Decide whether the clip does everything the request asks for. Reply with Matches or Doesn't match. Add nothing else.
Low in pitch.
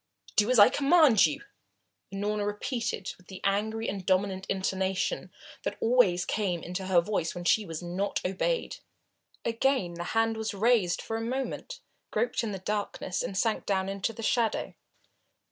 Doesn't match